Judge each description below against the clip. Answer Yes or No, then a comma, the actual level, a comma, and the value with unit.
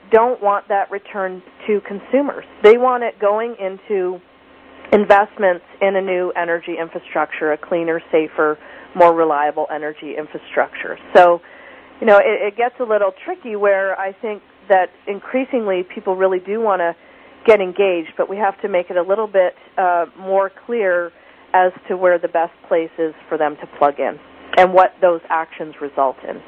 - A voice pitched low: No, high, 190 Hz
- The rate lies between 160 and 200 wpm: Yes, average, 170 wpm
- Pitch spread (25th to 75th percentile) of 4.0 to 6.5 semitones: No, average, 3.4 semitones